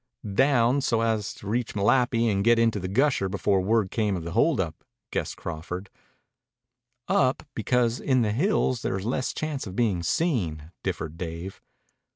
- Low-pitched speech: Yes, low, 110 Hz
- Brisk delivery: No, average, 165 wpm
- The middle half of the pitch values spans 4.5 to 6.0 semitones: Yes, average, 4.8 semitones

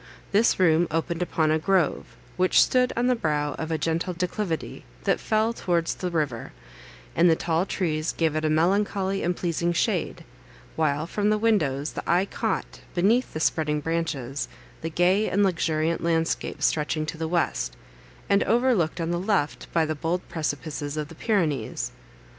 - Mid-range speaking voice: Yes, medium, 165 Hz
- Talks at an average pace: Yes, average, 170 wpm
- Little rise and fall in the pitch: No, average, 3.3 semitones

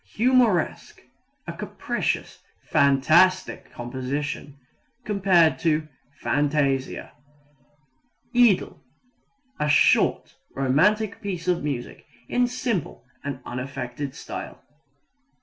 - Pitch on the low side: No, medium, 150 Hz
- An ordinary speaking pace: No, slow, 75 wpm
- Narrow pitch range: No, wide, 6.0 semitones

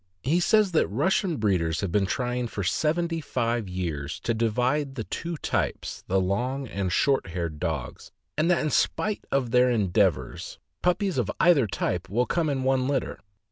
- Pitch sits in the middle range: No, low, 125 Hz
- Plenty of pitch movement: Yes, wide, 7.5 semitones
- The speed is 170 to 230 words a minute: Yes, average, 175 wpm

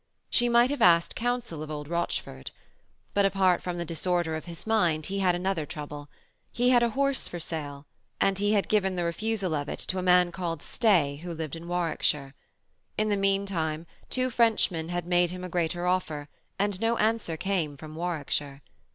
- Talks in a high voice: No, medium, 175 Hz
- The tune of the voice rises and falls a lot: No, average, 3.9 semitones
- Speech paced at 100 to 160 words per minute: No, average, 190 wpm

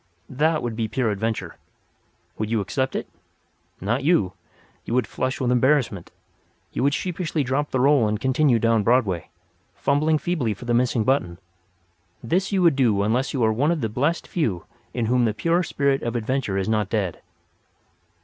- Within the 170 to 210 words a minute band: Yes, average, 180 wpm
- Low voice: Yes, low, 125 Hz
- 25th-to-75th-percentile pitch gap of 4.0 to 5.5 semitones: Yes, average, 4.6 semitones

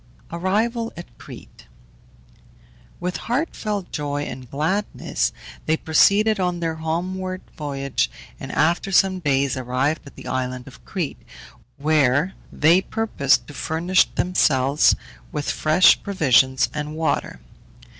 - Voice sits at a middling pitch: Yes, medium, 160 Hz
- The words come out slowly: Yes, slow, 115 wpm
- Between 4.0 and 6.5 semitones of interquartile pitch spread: Yes, average, 5.0 semitones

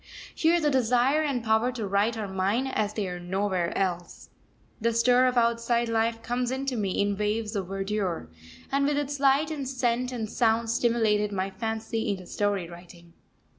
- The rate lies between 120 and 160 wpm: No, average, 175 wpm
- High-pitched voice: Yes, high, 225 Hz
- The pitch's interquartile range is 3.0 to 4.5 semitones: Yes, average, 3.8 semitones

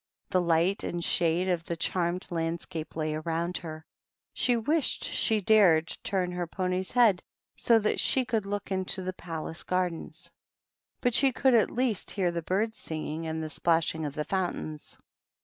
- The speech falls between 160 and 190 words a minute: Yes, average, 175 wpm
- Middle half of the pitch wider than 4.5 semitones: No, average, 3.8 semitones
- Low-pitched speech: No, medium, 180 Hz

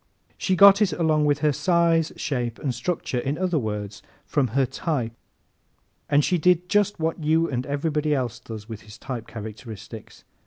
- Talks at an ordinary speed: Yes, average, 170 wpm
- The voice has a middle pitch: Yes, medium, 145 Hz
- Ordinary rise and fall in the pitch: No, wide, 5.7 semitones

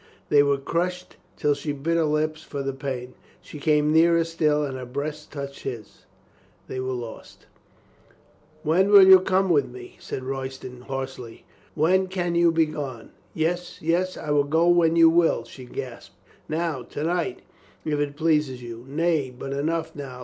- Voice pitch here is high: No, medium, 150 Hz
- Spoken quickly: No, average, 175 wpm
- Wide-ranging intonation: No, average, 3.8 semitones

